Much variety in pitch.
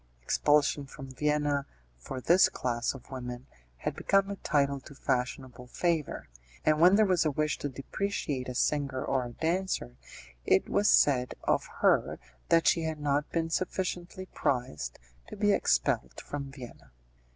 No: average, 4.4 semitones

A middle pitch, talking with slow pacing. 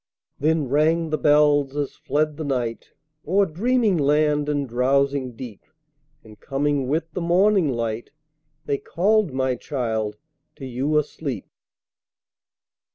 Yes: medium, 145 Hz; slow, 125 wpm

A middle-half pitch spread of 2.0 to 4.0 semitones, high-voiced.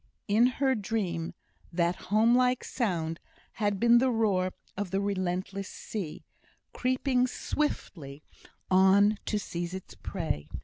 No: average, 4.6 semitones; high, 200 Hz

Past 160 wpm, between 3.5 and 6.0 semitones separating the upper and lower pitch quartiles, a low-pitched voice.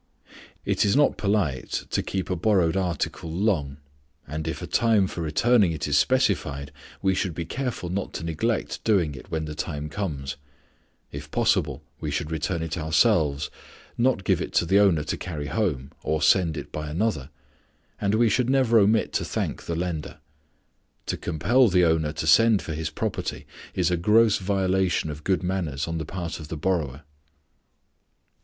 Yes: average, 175 wpm; average, 4.7 semitones; very low, 85 Hz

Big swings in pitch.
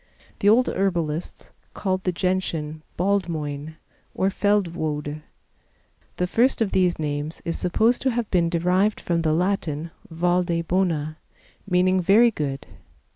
No: average, 3.5 semitones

